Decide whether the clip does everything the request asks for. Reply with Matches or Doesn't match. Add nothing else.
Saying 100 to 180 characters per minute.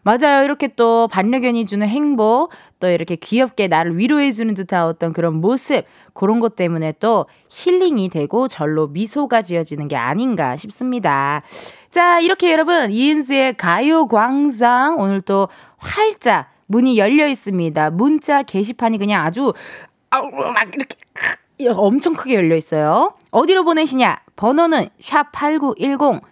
Doesn't match